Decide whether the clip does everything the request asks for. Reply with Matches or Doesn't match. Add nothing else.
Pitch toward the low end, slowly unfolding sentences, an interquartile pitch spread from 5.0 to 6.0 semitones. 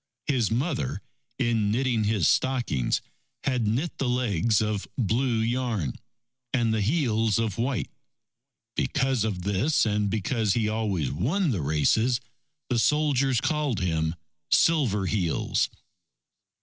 Doesn't match